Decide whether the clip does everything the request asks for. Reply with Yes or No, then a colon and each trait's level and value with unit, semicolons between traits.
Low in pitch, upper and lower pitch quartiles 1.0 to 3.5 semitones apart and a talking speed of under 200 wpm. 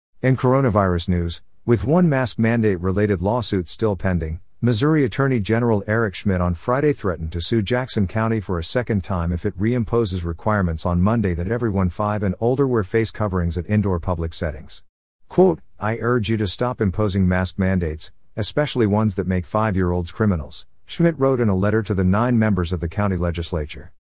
No: low, 105 Hz; average, 4.2 semitones; average, 180 wpm